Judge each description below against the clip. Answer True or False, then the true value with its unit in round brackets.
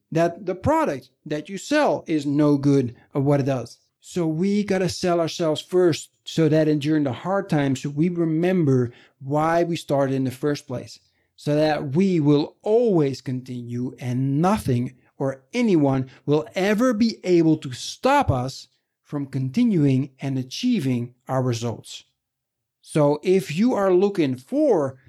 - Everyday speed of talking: True (155 wpm)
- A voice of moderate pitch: True (145 Hz)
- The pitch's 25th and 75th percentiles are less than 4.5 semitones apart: False (5.1 semitones)